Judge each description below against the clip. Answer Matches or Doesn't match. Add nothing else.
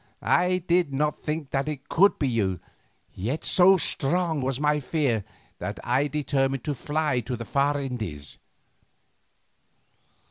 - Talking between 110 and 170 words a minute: Matches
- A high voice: Doesn't match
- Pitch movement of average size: Matches